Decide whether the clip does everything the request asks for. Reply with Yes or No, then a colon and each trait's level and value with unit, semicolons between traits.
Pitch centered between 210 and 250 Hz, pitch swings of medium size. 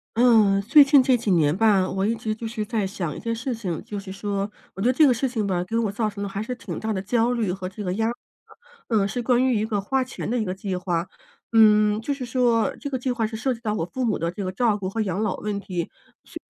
Yes: high, 215 Hz; average, 3.2 semitones